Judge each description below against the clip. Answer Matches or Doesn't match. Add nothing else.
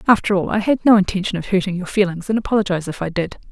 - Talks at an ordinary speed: Doesn't match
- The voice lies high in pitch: Matches